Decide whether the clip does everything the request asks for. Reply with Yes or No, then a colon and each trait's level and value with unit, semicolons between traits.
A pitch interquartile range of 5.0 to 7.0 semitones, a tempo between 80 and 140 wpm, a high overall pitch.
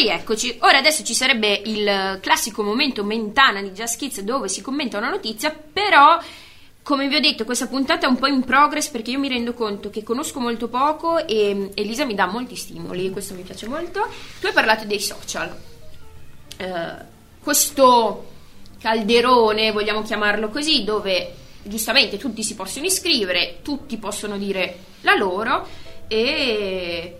No: wide, 5.4 semitones; average, 155 wpm; high, 230 Hz